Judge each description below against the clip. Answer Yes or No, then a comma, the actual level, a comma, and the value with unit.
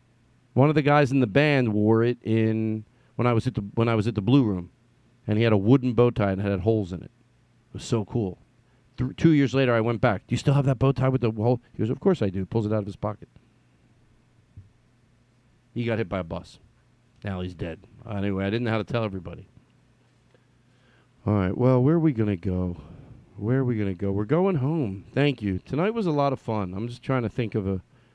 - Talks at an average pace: No, fast, 250 wpm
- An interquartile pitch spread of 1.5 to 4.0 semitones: Yes, average, 3.5 semitones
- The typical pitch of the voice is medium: No, low, 120 Hz